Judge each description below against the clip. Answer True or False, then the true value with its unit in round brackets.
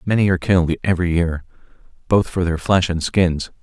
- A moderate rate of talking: True (180 wpm)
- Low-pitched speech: True (85 Hz)